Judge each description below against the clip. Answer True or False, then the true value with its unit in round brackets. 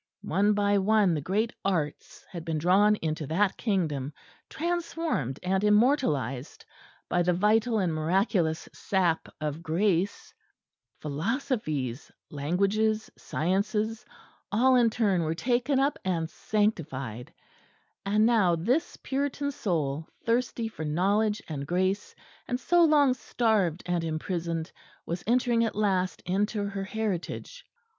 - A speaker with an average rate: False (120 wpm)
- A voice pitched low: False (195 Hz)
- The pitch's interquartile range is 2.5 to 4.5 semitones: False (5.3 semitones)